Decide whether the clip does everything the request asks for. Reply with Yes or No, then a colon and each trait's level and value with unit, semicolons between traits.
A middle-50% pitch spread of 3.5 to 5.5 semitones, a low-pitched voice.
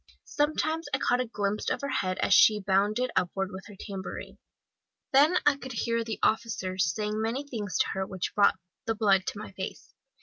No: average, 4.4 semitones; high, 210 Hz